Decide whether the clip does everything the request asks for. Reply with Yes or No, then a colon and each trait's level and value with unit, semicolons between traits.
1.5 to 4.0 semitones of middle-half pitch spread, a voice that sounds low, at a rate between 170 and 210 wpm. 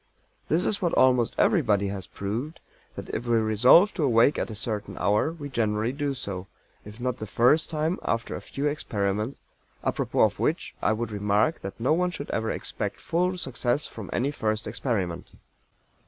No: wide, 5.5 semitones; low, 120 Hz; average, 180 wpm